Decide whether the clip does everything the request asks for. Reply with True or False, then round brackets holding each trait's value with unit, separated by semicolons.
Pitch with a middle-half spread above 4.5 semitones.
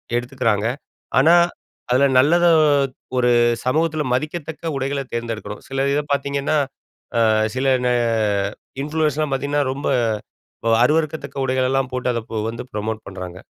False (3.6 semitones)